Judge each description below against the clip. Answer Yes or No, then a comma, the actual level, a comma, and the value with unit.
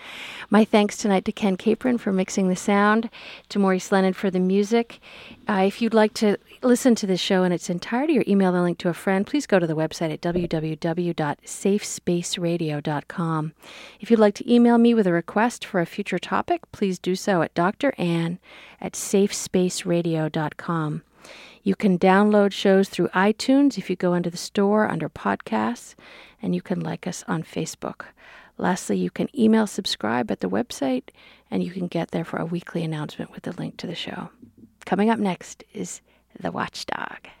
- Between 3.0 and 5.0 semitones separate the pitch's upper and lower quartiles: Yes, average, 3.8 semitones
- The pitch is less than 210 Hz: Yes, high, 190 Hz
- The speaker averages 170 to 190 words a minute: Yes, average, 180 wpm